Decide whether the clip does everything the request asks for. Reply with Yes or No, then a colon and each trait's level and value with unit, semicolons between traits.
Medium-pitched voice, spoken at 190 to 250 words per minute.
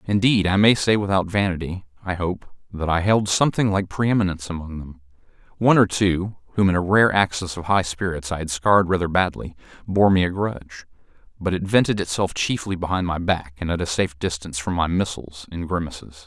No: very low, 90 Hz; average, 195 wpm